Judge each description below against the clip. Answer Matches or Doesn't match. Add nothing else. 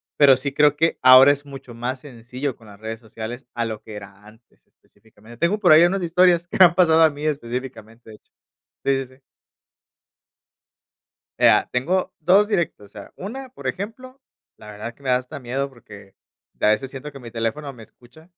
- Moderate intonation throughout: Doesn't match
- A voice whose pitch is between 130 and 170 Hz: Matches